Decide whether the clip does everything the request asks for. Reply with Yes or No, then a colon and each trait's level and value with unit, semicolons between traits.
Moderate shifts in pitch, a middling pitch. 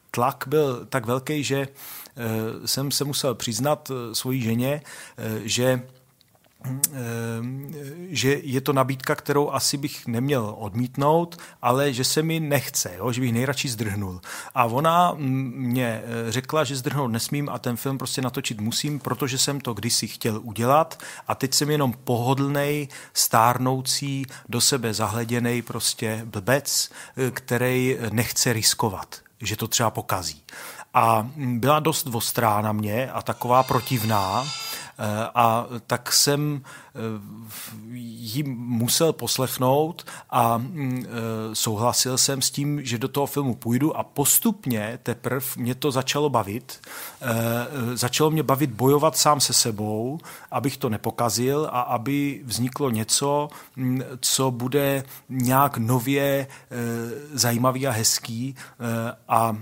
No: average, 3.1 semitones; low, 130 Hz